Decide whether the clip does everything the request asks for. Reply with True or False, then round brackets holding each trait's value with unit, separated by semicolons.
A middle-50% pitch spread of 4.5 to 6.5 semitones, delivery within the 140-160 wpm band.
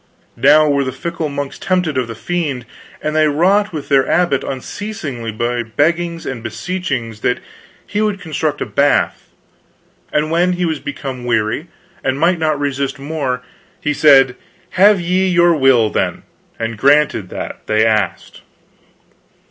True (5.1 semitones; 150 wpm)